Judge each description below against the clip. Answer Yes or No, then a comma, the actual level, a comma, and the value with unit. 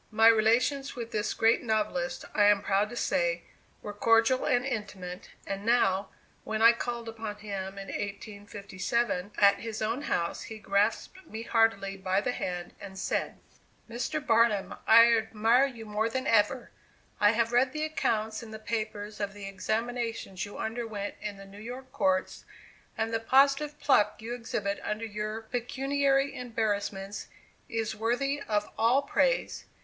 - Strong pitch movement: No, average, 2.8 semitones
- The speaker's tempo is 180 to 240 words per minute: No, average, 155 wpm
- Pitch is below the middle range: No, high, 225 Hz